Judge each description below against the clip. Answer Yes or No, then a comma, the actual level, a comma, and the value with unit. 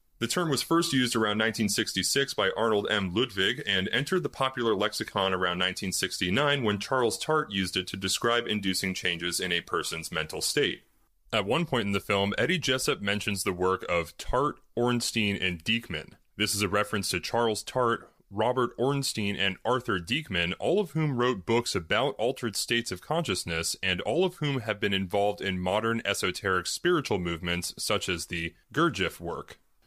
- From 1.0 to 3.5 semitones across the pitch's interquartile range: No, average, 4.6 semitones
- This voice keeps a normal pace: Yes, average, 175 wpm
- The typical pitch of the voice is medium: No, low, 105 Hz